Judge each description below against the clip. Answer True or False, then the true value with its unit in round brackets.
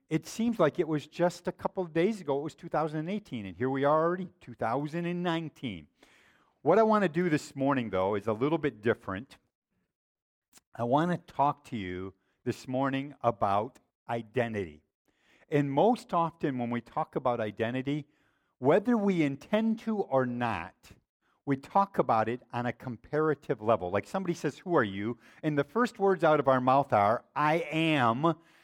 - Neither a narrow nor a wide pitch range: False (5.8 semitones)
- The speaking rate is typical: True (170 wpm)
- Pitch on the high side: False (145 Hz)